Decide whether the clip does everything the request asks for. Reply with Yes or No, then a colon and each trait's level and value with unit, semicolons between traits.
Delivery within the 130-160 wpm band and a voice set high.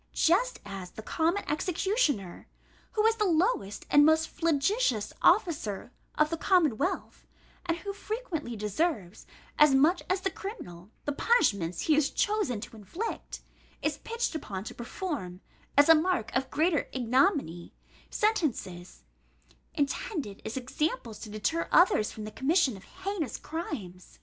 Yes: average, 140 wpm; very high, 300 Hz